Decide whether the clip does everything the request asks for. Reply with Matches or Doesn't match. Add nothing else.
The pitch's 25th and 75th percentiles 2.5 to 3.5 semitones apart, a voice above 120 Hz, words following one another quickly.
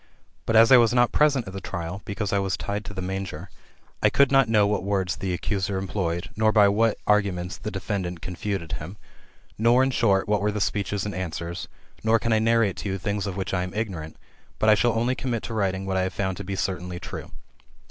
Doesn't match